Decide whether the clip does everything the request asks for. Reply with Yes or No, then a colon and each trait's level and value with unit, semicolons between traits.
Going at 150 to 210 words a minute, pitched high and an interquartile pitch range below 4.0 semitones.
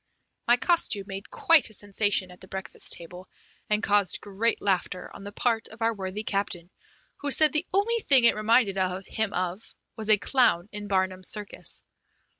Yes: average, 175 wpm; high, 205 Hz; average, 3.5 semitones